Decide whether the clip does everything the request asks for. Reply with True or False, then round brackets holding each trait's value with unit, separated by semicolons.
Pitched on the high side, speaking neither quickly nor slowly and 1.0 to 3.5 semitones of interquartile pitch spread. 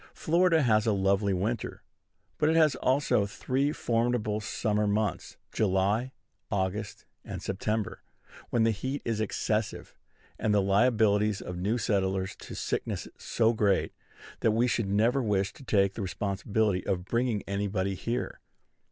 False (105 Hz; 145 wpm; 3.1 semitones)